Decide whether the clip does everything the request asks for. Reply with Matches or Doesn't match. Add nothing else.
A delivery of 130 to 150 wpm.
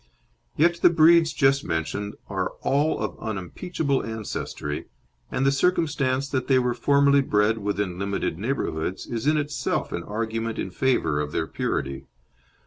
Matches